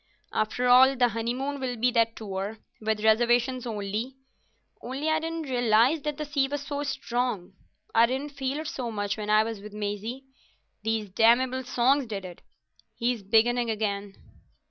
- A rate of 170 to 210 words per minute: No, average, 160 wpm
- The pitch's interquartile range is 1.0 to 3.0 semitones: No, average, 3.5 semitones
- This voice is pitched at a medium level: No, high, 240 Hz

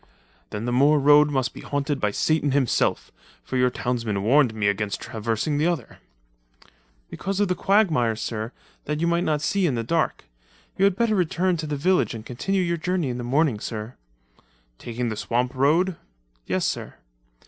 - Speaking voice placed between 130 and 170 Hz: Yes, medium, 140 Hz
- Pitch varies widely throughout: Yes, wide, 6.2 semitones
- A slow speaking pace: No, average, 180 wpm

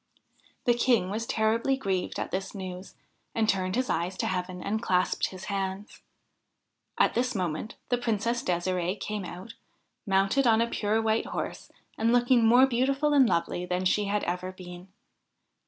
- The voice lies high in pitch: Yes, high, 205 Hz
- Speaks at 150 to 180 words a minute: Yes, average, 165 wpm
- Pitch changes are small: No, average, 4.2 semitones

